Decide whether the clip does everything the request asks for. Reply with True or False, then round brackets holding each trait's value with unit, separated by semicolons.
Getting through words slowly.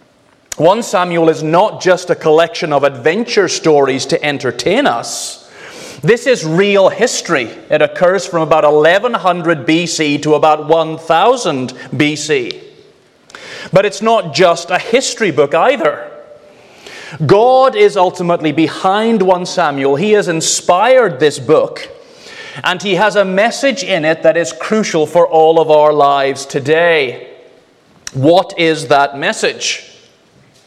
True (130 wpm)